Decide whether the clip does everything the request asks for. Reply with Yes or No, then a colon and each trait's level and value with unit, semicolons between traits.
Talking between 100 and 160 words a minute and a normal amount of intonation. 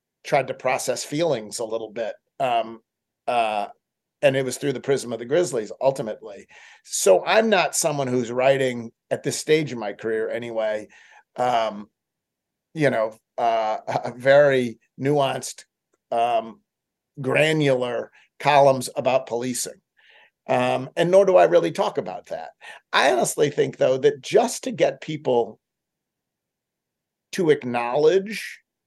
Yes: slow, 135 wpm; average, 4.3 semitones